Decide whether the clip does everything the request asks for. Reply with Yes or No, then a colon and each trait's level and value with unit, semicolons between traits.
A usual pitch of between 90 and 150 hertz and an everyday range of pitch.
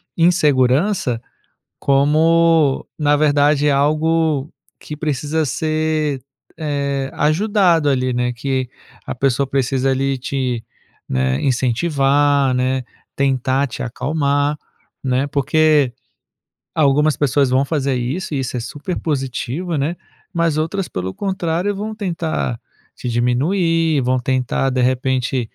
Yes: medium, 140 Hz; average, 3.3 semitones